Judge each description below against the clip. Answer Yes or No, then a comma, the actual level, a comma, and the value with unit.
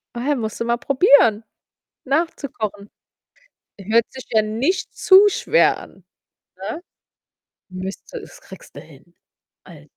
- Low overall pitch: No, high, 235 Hz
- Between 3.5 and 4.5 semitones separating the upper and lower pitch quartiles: No, average, 5.3 semitones